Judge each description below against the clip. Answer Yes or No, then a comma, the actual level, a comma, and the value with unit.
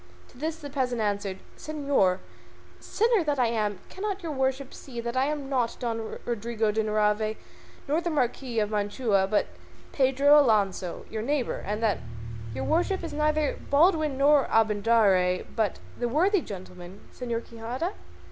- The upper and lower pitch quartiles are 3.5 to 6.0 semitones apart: Yes, wide, 5.5 semitones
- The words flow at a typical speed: Yes, average, 155 wpm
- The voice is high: Yes, high, 240 Hz